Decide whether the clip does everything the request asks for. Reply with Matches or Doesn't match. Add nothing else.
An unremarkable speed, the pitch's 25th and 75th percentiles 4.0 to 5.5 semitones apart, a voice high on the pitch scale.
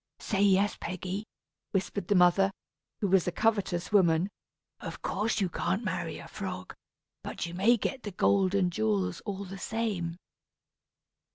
Doesn't match